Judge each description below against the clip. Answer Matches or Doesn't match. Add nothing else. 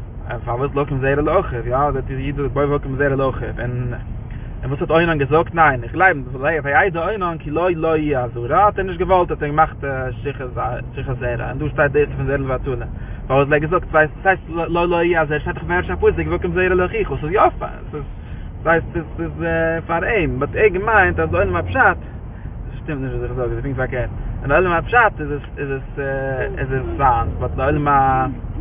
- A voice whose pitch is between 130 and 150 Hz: Matches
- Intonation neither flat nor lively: Matches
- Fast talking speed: Matches